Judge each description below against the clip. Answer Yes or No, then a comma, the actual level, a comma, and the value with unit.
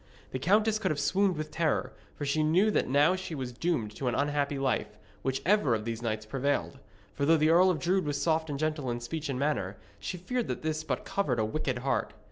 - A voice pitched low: No, medium, 150 Hz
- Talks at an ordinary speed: No, fast, 230 wpm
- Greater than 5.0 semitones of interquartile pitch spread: No, average, 4.3 semitones